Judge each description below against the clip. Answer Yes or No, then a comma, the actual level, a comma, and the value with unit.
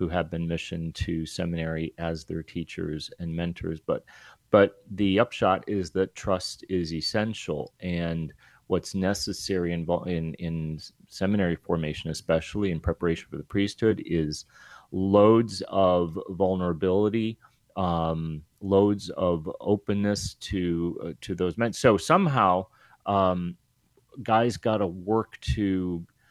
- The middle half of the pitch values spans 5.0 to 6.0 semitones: No, average, 3.1 semitones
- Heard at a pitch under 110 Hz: Yes, very low, 90 Hz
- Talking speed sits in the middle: No, slow, 125 wpm